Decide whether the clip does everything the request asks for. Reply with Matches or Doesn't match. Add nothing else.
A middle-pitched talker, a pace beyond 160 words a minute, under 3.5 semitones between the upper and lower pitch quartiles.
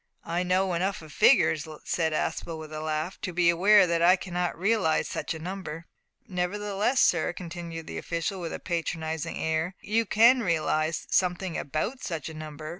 Matches